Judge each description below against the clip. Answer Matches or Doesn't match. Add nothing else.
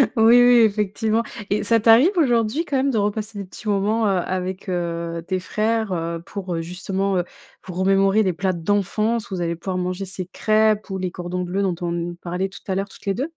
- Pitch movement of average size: Matches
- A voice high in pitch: Matches